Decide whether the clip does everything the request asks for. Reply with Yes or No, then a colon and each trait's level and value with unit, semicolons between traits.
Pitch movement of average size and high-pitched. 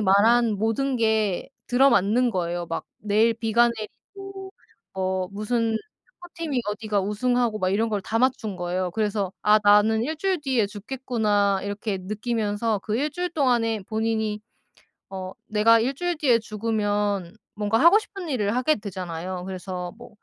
Yes: average, 3.3 semitones; high, 220 Hz